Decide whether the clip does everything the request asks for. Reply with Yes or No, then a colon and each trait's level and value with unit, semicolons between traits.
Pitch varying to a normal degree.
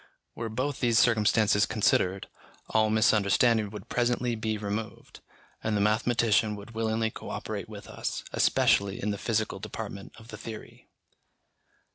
No: narrow, 1.7 semitones